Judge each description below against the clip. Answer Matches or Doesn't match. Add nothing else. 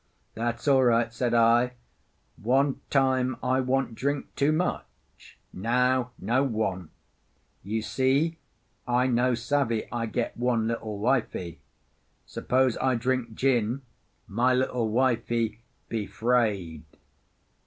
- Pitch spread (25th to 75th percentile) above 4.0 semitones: Doesn't match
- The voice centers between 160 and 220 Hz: Doesn't match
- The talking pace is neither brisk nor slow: Doesn't match